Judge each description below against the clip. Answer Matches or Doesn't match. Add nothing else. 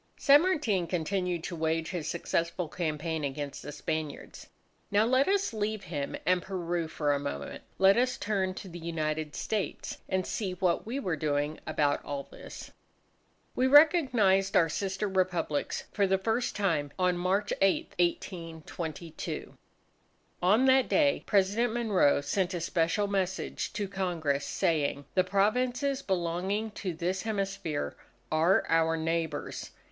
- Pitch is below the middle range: Doesn't match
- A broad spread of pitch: Doesn't match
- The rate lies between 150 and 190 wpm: Doesn't match